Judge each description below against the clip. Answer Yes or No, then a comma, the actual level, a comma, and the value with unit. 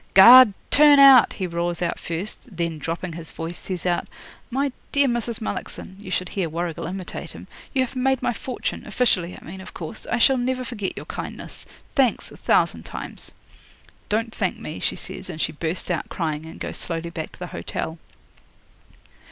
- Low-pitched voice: No, medium, 185 Hz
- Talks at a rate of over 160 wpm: Yes, average, 185 wpm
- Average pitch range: No, wide, 6.4 semitones